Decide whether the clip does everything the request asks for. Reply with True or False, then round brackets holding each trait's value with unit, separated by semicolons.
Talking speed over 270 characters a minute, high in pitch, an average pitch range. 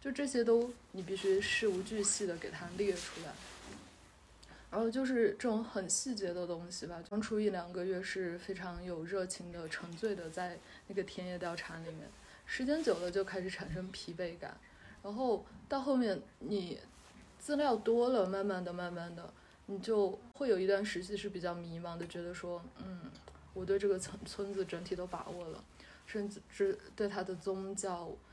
False (255 characters per minute; 195 Hz; 3.0 semitones)